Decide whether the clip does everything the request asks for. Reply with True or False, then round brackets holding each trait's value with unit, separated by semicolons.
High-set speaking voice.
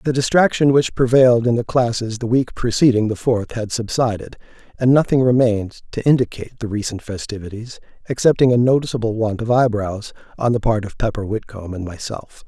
False (115 Hz)